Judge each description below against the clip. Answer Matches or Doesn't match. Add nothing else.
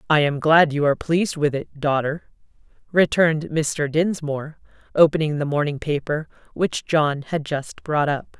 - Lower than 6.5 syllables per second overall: Matches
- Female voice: Matches